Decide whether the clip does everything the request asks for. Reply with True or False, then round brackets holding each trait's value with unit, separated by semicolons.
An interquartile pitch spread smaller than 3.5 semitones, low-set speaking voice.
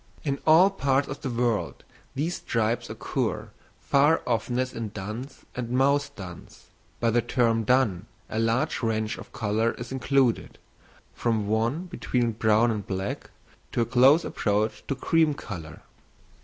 False (3.8 semitones; 120 Hz)